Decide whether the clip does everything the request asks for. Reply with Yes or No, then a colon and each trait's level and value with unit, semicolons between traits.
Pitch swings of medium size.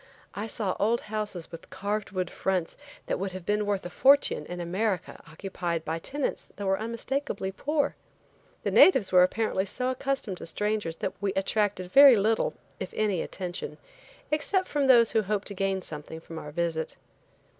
Yes: average, 3.8 semitones